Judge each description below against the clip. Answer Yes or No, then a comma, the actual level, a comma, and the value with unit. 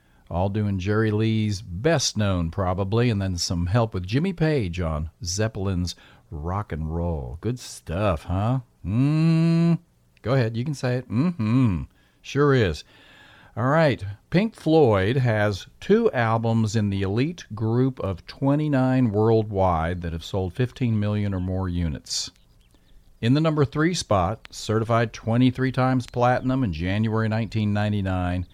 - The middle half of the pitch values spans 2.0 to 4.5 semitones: No, wide, 5.5 semitones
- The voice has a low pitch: Yes, low, 110 Hz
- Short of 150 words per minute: Yes, average, 140 wpm